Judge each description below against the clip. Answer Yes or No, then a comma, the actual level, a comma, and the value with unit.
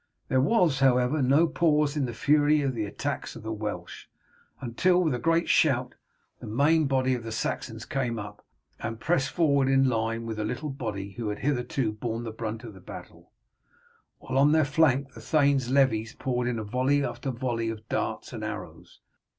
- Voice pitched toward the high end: No, low, 130 Hz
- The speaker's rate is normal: Yes, average, 190 wpm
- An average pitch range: Yes, average, 3.9 semitones